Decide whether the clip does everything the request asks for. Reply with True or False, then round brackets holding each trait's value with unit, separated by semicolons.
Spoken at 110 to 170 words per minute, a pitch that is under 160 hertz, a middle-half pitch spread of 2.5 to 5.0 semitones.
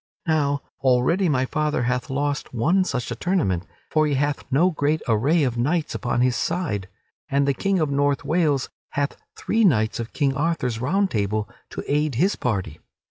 False (185 wpm; 140 Hz; 4.3 semitones)